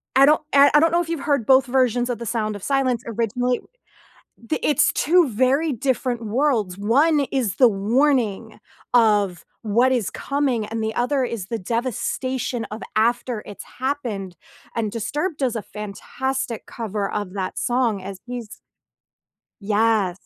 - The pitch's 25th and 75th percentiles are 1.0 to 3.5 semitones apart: No, average, 4.0 semitones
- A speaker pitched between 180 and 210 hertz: No, high, 240 Hz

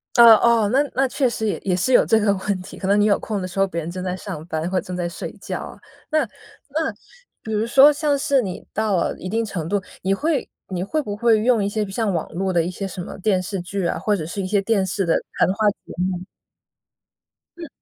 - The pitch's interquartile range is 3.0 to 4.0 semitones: Yes, average, 3.7 semitones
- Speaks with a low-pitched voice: No, high, 200 Hz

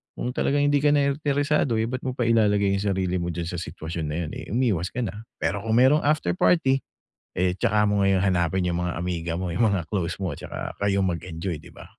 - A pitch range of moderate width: No, wide, 5.7 semitones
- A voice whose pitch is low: Yes, low, 100 Hz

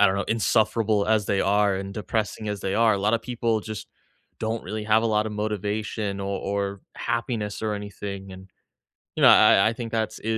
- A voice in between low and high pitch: No, low, 105 Hz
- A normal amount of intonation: No, narrow, 1.8 semitones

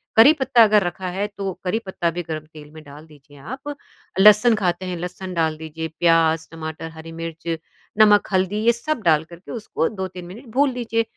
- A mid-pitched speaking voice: Yes, medium, 180 Hz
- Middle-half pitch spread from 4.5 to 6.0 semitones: Yes, average, 4.8 semitones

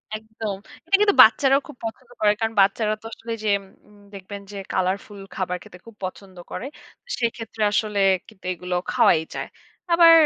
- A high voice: Yes, high, 215 Hz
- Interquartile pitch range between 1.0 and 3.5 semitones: Yes, narrow, 2.5 semitones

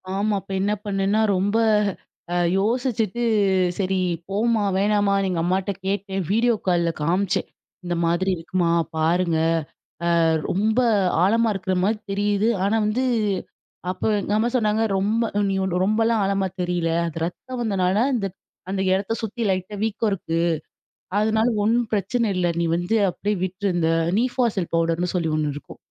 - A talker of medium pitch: No, high, 195 Hz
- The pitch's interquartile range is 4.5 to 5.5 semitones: No, average, 3.2 semitones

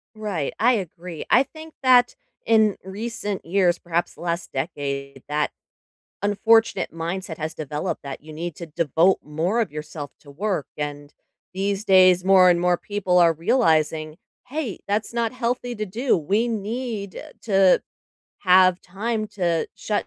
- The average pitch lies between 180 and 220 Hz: Yes, medium, 185 Hz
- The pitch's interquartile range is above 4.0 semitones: Yes, average, 5.0 semitones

